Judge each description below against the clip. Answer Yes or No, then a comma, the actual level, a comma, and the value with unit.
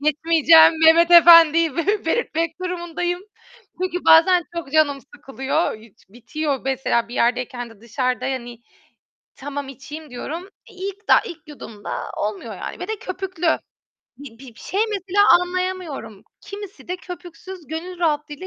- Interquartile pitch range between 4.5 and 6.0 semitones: Yes, average, 5.0 semitones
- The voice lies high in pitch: Yes, very high, 320 Hz